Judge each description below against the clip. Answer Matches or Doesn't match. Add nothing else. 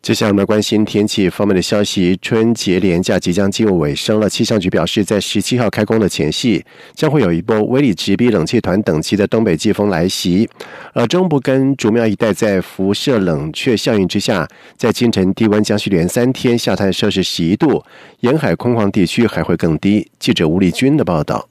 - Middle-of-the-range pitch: Doesn't match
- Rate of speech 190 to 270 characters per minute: Doesn't match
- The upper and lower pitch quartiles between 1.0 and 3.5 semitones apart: Matches